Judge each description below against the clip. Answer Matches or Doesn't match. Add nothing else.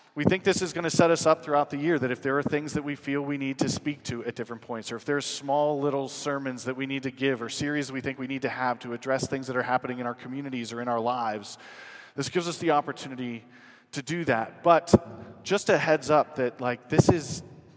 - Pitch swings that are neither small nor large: Matches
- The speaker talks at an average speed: Doesn't match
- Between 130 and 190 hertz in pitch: Matches